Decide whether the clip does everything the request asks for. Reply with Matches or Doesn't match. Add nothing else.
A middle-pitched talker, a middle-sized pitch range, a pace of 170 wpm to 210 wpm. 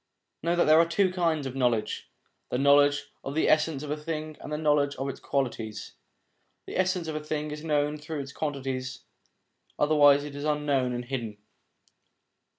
Doesn't match